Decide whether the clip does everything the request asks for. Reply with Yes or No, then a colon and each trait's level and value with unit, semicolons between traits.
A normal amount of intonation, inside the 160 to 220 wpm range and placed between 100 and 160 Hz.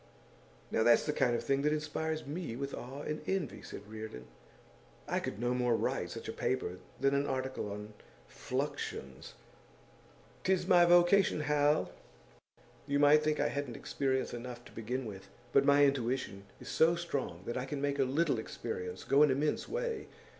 Yes: average, 4.1 semitones; average, 175 wpm; medium, 140 Hz